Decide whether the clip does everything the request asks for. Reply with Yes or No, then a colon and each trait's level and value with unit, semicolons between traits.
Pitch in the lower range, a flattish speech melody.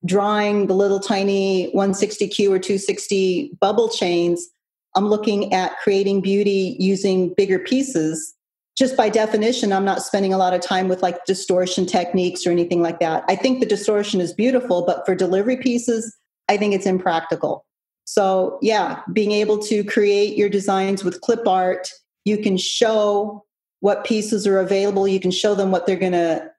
No: high, 195 Hz; narrow, 2.1 semitones